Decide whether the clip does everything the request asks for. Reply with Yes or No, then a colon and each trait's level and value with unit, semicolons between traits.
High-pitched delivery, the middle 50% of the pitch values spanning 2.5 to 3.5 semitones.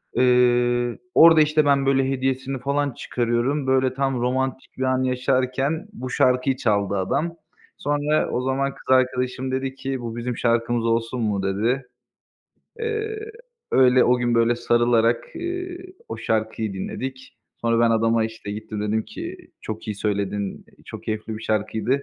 No: low, 125 Hz; average, 2.9 semitones